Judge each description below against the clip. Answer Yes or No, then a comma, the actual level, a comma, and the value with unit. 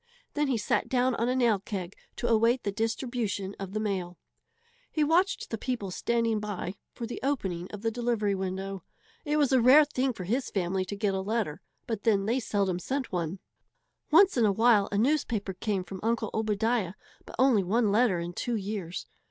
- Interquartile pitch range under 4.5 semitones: Yes, average, 3.9 semitones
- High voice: Yes, high, 215 Hz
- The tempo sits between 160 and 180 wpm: No, average, 195 wpm